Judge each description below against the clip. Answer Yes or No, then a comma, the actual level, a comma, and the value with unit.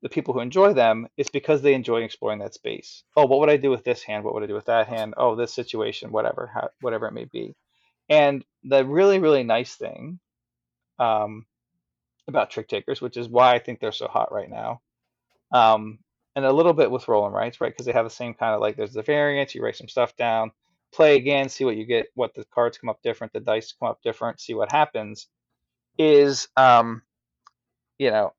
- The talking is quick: Yes, fast, 220 wpm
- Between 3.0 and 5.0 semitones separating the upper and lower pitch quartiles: Yes, average, 4.1 semitones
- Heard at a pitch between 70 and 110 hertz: No, low, 120 Hz